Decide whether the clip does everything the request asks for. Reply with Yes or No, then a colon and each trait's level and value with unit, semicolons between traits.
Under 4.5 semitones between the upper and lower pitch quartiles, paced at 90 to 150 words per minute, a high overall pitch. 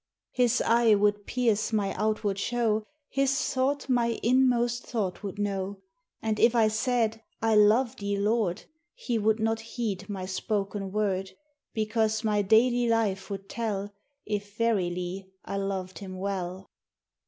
Yes: average, 2.8 semitones; average, 140 wpm; high, 215 Hz